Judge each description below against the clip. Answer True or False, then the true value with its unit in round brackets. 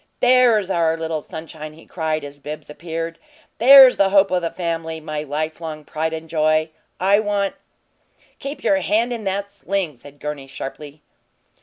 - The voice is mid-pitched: True (165 Hz)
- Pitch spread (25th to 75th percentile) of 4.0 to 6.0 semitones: True (4.4 semitones)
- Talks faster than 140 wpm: True (165 wpm)